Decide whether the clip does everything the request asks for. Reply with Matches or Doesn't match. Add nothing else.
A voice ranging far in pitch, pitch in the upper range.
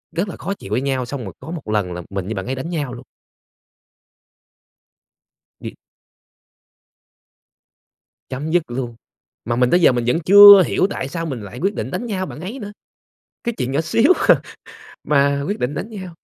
Doesn't match